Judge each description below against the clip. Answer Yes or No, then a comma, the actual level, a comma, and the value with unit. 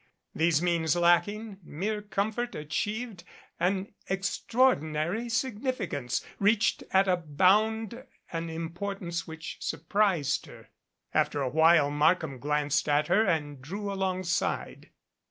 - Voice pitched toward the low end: No, medium, 180 Hz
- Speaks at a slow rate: Yes, slow, 110 wpm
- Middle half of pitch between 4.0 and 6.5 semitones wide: Yes, average, 4.7 semitones